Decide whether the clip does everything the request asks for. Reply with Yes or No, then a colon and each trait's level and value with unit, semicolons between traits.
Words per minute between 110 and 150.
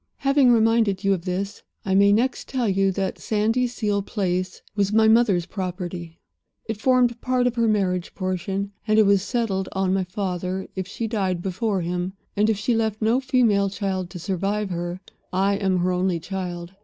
No: average, 180 wpm